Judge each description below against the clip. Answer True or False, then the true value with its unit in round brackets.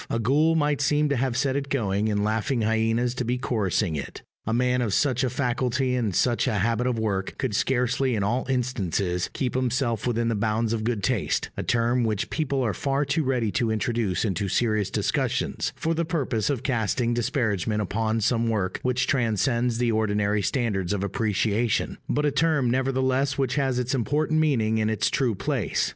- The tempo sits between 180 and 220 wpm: True (190 wpm)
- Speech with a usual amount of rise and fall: True (3.4 semitones)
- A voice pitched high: False (120 Hz)